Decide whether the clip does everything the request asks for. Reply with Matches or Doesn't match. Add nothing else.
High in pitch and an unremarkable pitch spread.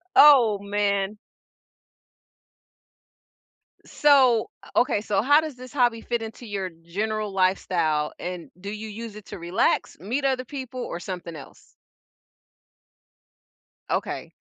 Matches